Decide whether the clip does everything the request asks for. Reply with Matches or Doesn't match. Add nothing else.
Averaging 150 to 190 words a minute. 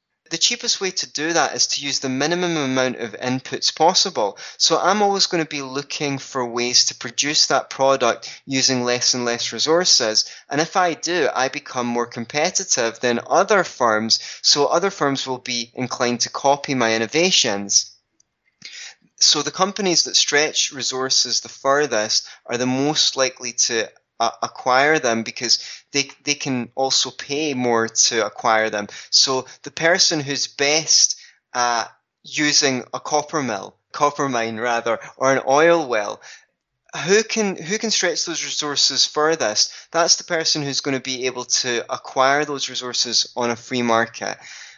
Matches